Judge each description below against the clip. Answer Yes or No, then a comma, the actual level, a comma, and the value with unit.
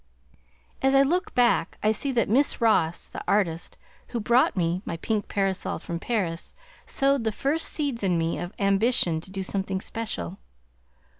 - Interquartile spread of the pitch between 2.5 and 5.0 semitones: No, wide, 5.6 semitones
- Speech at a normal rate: Yes, average, 165 wpm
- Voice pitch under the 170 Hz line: No, high, 205 Hz